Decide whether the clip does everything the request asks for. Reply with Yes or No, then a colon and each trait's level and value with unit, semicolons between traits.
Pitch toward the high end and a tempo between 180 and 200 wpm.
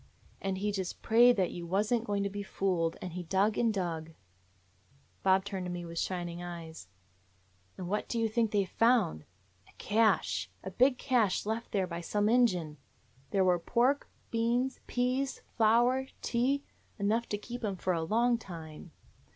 Yes: high, 200 Hz; average, 185 wpm